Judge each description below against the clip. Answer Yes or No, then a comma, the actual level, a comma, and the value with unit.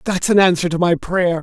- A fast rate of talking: Yes, fast, 255 wpm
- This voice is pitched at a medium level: Yes, medium, 175 Hz